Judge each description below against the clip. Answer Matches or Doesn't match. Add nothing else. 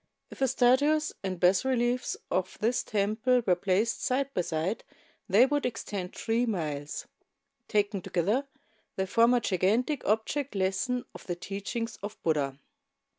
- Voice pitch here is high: Matches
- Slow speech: Doesn't match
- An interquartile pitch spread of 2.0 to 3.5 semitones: Doesn't match